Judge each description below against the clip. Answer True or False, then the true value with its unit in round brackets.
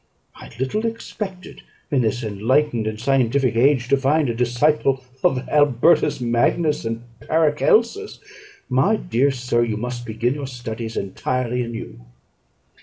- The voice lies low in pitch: True (125 Hz)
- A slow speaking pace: True (130 wpm)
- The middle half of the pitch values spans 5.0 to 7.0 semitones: False (3.9 semitones)